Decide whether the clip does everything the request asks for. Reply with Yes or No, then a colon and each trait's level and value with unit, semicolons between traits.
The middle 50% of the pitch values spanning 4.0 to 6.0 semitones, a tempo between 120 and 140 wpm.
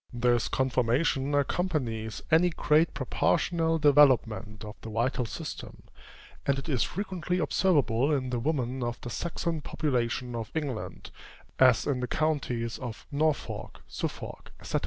Yes: average, 4.5 semitones; slow, 135 wpm